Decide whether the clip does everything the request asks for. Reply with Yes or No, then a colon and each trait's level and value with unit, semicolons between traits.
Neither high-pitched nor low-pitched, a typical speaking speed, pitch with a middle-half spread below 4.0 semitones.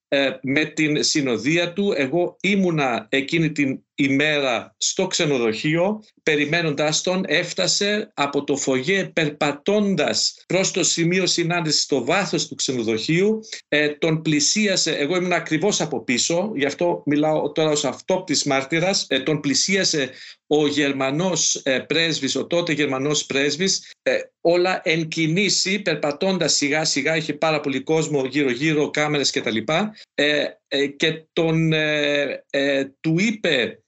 Yes: medium, 155 Hz; average, 135 wpm; average, 3.6 semitones